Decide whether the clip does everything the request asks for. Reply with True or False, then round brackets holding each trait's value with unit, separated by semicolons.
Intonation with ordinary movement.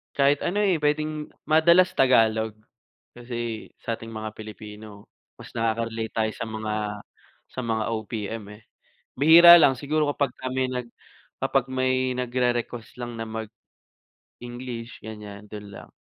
True (3.7 semitones)